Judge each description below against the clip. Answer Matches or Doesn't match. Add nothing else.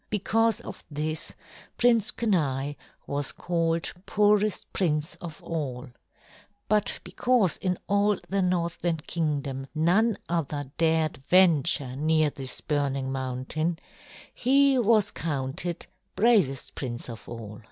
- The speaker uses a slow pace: Matches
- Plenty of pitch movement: Matches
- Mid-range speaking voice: Matches